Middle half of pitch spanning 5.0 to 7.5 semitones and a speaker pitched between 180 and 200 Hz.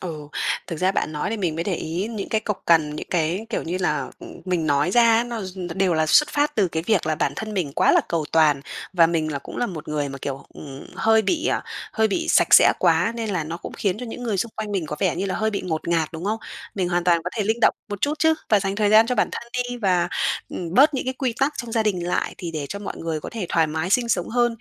Yes: average, 5.3 semitones; medium, 185 Hz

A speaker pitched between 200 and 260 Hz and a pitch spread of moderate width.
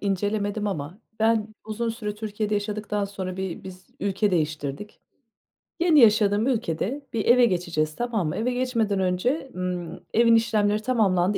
Yes: high, 210 Hz; average, 3.6 semitones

